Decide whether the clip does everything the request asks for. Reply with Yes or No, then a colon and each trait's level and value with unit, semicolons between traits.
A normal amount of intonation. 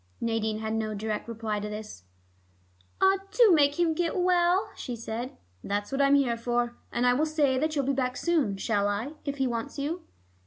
No: wide, 5.7 semitones